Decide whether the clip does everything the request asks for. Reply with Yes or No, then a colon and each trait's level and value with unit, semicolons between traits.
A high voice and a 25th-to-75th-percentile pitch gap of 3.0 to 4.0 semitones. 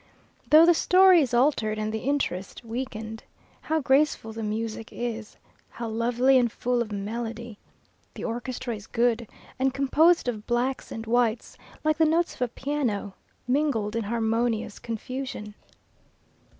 Yes: high, 240 Hz; average, 3.3 semitones